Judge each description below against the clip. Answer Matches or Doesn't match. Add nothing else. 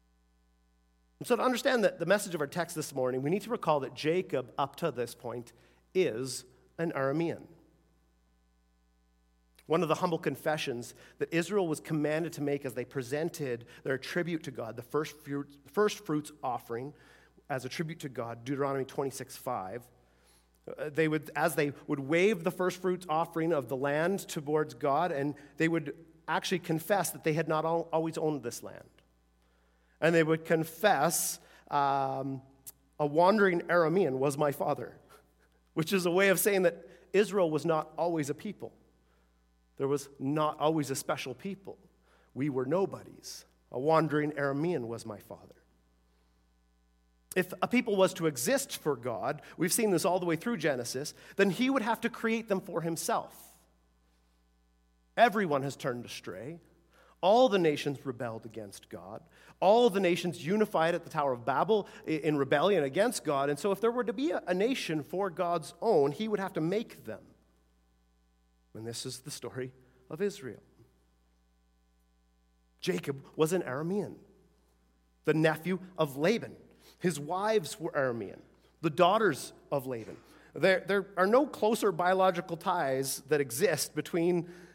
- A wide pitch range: Matches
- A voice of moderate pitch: Matches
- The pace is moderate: Matches